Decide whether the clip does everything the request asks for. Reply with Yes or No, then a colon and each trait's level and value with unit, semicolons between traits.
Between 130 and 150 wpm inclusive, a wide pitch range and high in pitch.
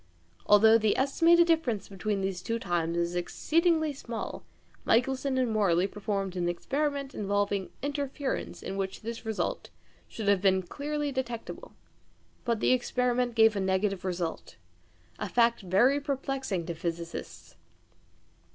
Yes: slow, 135 wpm; wide, 5.8 semitones; high, 220 Hz